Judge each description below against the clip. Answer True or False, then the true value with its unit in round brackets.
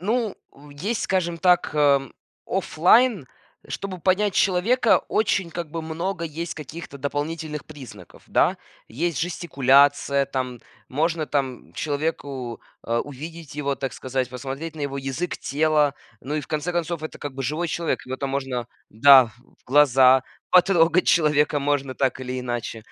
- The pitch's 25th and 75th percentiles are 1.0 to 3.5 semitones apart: False (3.9 semitones)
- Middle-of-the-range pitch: True (150 Hz)